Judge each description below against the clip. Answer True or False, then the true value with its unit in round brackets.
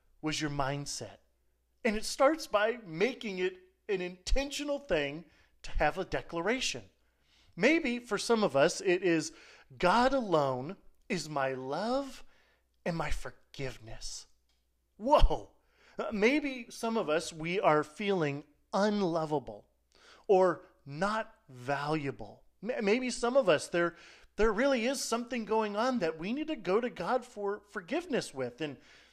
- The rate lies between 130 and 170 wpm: True (135 wpm)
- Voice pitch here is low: False (190 Hz)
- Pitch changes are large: True (7.4 semitones)